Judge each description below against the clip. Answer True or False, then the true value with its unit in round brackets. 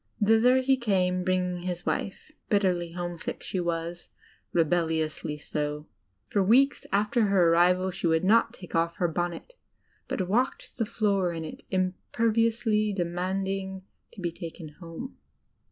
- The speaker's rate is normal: True (150 wpm)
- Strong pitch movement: False (3.4 semitones)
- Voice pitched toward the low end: False (185 Hz)